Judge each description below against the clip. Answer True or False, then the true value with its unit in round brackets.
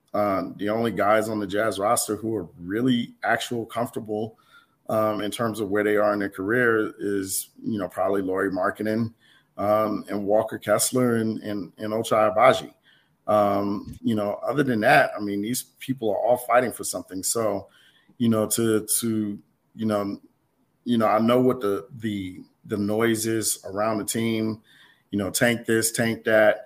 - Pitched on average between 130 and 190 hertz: False (110 Hz)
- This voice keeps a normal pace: True (175 wpm)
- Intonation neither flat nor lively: False (1.8 semitones)